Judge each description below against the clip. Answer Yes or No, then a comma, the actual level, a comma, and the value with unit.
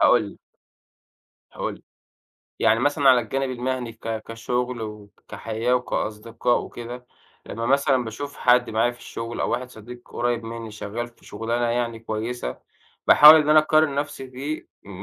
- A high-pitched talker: No, low, 120 Hz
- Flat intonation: Yes, narrow, 2.2 semitones